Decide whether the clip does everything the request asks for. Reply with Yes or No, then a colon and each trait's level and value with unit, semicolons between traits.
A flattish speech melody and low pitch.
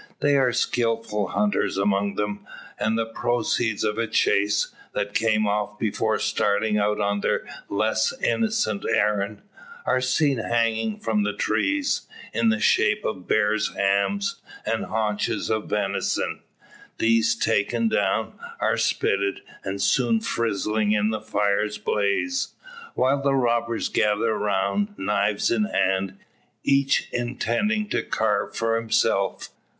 Yes: narrow, 2.3 semitones; low, 110 Hz